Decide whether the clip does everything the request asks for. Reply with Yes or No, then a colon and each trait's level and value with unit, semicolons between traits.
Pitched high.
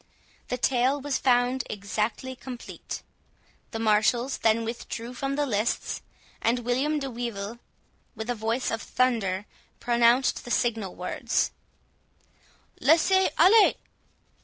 Yes: high, 240 Hz